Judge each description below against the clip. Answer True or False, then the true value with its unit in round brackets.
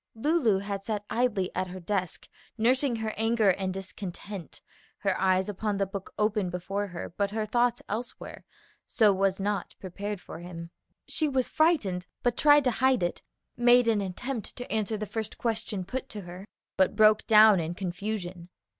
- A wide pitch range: False (3.3 semitones)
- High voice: True (205 Hz)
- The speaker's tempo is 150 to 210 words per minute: True (170 wpm)